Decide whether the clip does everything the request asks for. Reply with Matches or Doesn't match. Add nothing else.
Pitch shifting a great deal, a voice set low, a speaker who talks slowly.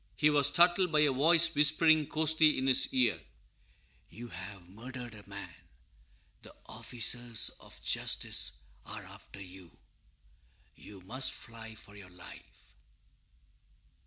Matches